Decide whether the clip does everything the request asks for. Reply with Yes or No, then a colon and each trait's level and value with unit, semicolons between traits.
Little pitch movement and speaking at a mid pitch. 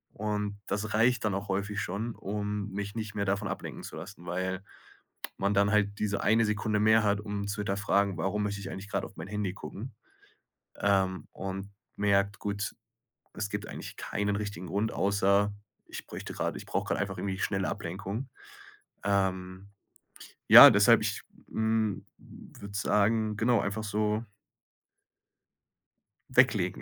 No: narrow, 1.1 semitones; low, 100 Hz